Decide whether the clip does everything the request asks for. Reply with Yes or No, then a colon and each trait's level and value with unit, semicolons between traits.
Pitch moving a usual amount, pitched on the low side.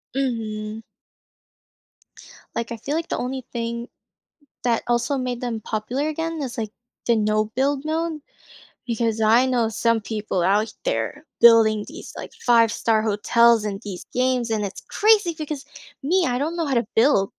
No: average, 4.0 semitones; high, 235 Hz